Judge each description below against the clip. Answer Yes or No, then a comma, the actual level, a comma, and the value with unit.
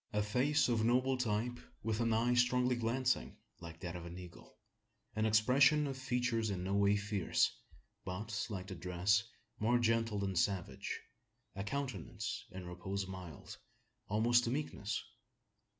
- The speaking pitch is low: Yes, low, 110 Hz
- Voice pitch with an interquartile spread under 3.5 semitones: No, average, 4.1 semitones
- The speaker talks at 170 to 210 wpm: No, average, 150 wpm